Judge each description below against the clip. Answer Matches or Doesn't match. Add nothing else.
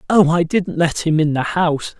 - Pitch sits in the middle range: Matches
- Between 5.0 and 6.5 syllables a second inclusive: Matches